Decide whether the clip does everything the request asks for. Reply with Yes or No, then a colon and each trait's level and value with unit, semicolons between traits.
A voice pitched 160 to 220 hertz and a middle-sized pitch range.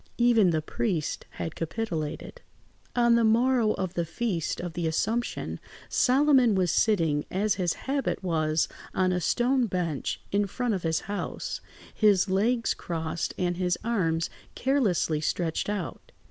No: high, 190 Hz; wide, 5.8 semitones